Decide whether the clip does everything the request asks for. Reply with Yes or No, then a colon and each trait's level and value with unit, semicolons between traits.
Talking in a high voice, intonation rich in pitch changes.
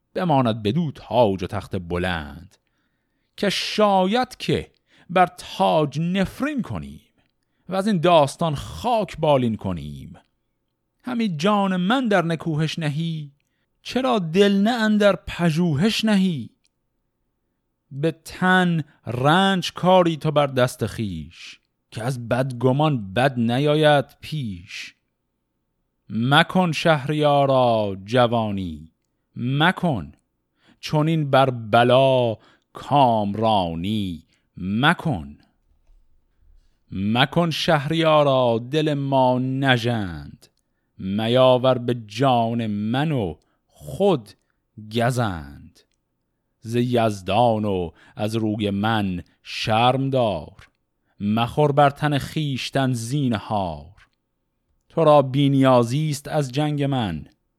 No: low, 130 Hz; wide, 7.2 semitones